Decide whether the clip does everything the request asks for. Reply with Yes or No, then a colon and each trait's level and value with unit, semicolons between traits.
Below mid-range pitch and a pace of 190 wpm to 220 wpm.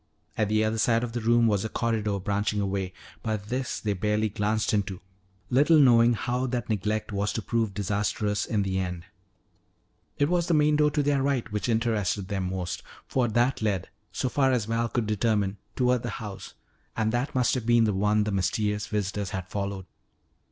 Yes: low, 110 Hz; average, 195 wpm